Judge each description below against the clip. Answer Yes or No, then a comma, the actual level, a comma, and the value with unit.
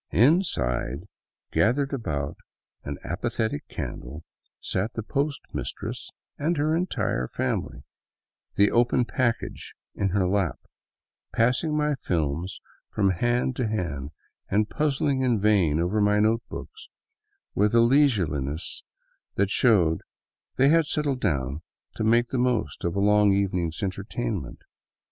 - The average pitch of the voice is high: No, low, 105 Hz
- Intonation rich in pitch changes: Yes, wide, 6.4 semitones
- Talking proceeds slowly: Yes, slow, 125 wpm